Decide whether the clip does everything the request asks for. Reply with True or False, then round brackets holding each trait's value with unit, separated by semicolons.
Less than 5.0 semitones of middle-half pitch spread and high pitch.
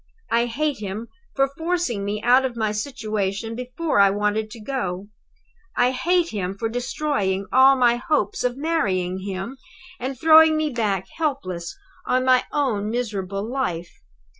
False (5.3 semitones; 235 Hz)